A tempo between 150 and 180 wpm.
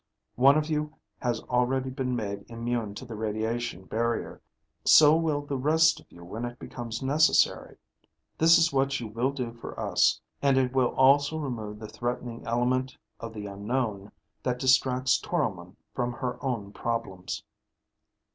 Yes: average, 155 wpm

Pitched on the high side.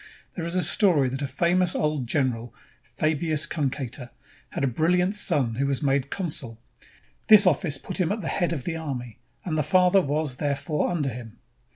No: medium, 150 Hz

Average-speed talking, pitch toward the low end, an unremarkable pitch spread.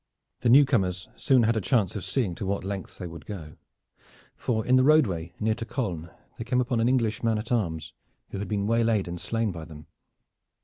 No: fast, 215 wpm; low, 110 Hz; average, 4.6 semitones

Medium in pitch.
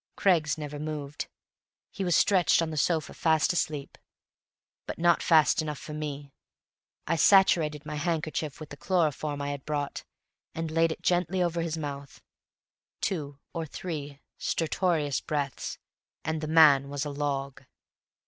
Yes: medium, 155 Hz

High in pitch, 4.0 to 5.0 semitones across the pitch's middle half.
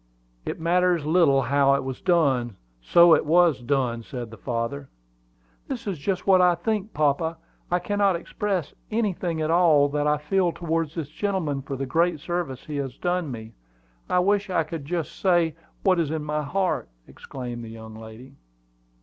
No: medium, 160 Hz; average, 4.6 semitones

